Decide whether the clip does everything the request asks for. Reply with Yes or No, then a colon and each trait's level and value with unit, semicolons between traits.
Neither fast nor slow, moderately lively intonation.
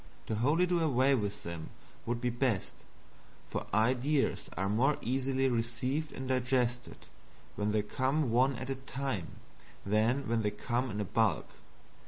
Yes: average, 150 wpm; average, 3.4 semitones